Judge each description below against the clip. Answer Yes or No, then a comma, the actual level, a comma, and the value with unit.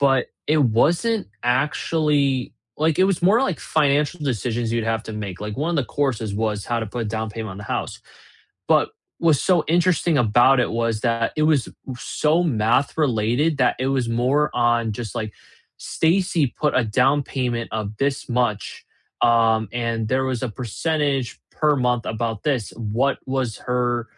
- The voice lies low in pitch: Yes, low, 125 Hz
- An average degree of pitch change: Yes, average, 4.6 semitones